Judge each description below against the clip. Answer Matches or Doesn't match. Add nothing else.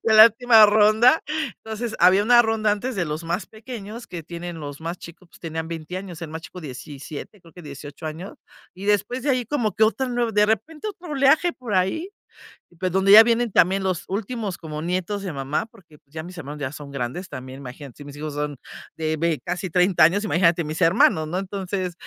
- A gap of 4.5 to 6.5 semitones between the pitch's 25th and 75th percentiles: Matches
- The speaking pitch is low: Doesn't match